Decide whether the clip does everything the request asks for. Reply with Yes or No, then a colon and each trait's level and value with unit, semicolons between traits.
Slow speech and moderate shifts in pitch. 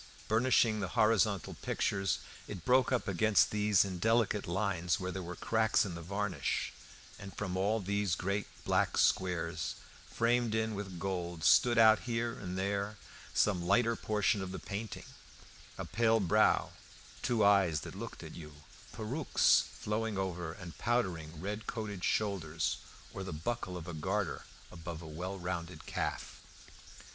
No: average, 155 wpm; average, 3.6 semitones